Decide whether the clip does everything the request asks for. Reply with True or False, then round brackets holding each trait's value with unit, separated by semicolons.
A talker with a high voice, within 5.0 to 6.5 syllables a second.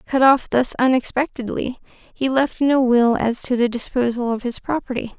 False (250 Hz; 4.7 syllables/s)